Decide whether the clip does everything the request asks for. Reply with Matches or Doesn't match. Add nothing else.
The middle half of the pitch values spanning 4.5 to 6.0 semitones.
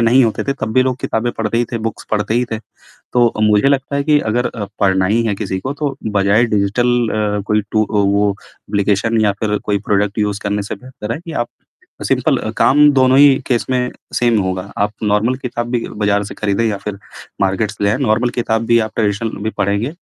Doesn't match